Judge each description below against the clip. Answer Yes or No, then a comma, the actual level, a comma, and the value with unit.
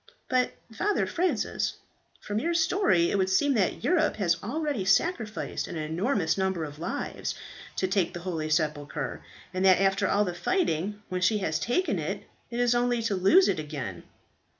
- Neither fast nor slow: Yes, average, 175 wpm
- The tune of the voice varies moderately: No, wide, 6.3 semitones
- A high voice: Yes, high, 195 Hz